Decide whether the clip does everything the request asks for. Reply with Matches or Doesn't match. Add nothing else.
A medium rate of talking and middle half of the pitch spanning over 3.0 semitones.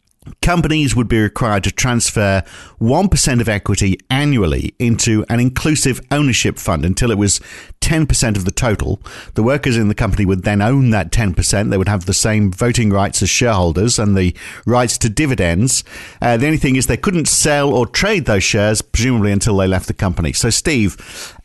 Matches